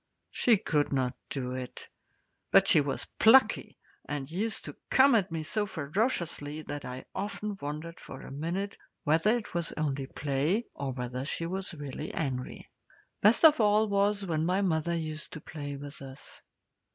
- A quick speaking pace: No, average, 165 wpm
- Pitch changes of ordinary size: No, wide, 5.8 semitones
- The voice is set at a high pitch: No, medium, 160 Hz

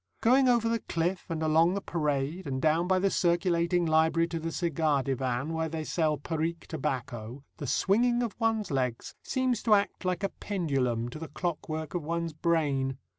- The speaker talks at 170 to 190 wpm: Yes, average, 180 wpm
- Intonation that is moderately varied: Yes, average, 3.9 semitones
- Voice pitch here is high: No, medium, 165 Hz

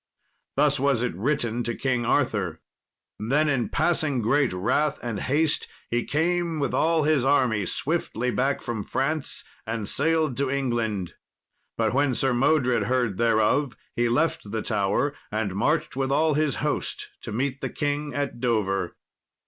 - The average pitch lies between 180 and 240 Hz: No, low, 130 Hz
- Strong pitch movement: No, average, 4.4 semitones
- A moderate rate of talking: Yes, average, 155 wpm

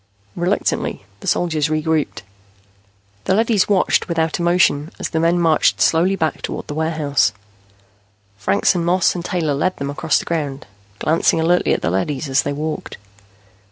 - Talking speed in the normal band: Yes, average, 160 wpm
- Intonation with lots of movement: No, average, 3.1 semitones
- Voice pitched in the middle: Yes, medium, 160 Hz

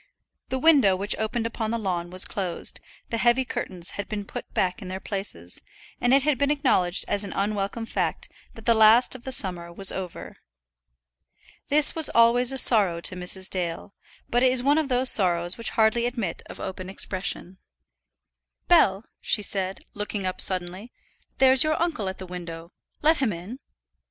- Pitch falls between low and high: No, high, 205 Hz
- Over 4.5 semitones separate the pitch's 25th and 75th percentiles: Yes, average, 4.9 semitones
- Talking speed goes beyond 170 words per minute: Yes, average, 180 wpm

